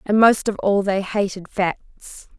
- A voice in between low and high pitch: No, high, 200 Hz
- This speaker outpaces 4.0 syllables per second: No, 3.6 syllables/s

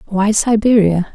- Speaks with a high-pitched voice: Yes, high, 205 Hz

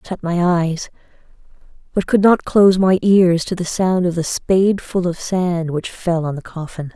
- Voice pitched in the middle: Yes, medium, 175 Hz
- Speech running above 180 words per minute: Yes, average, 200 wpm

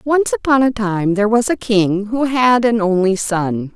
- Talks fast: Yes, fast, 210 wpm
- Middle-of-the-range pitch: No, high, 220 Hz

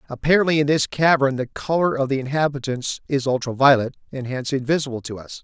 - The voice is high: No, low, 135 Hz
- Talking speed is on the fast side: No, average, 190 wpm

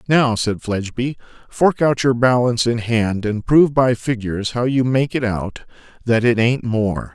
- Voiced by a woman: No, male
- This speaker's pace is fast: No, average, 185 wpm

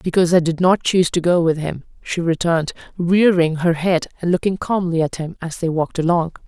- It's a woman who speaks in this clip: Yes, female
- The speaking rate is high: Yes, fast, 215 wpm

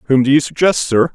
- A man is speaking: Yes, male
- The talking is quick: Yes, fast, 260 wpm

